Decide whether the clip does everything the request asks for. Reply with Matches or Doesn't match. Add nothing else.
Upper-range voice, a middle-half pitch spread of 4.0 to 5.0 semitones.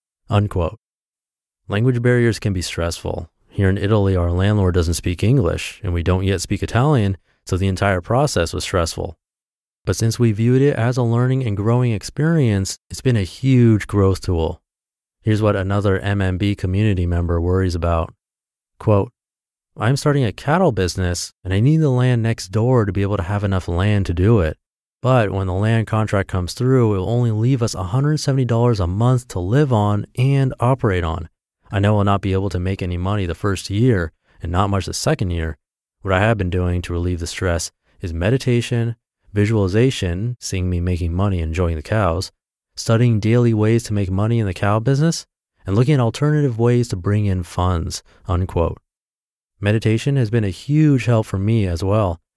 Doesn't match